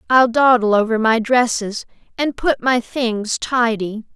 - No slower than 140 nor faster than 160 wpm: Yes, average, 145 wpm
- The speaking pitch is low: No, high, 235 Hz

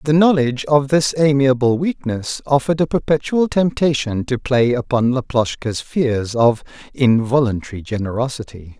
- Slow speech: Yes, slow, 125 wpm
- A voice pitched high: No, low, 130 Hz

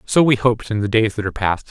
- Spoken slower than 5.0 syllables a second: No, 7.0 syllables/s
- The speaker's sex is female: No, male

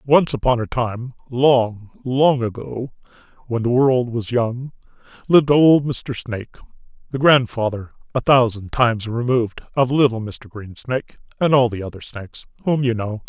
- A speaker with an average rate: Yes, average, 155 wpm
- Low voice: Yes, low, 120 Hz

